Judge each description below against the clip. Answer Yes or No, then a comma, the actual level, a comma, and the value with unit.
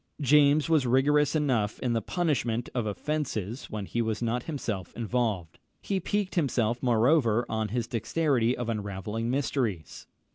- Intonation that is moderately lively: Yes, average, 4.7 semitones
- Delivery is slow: No, average, 145 wpm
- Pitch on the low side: Yes, low, 120 Hz